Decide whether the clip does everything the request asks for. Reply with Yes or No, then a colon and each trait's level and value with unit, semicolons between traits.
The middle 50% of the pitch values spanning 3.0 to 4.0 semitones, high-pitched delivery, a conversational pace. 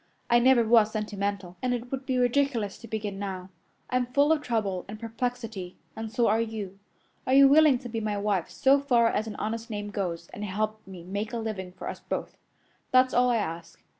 No: average, 3.6 semitones; high, 220 Hz; fast, 210 wpm